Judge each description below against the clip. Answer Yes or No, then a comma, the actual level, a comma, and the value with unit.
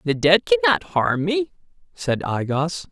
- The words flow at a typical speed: Yes, average, 165 wpm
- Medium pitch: Yes, medium, 150 Hz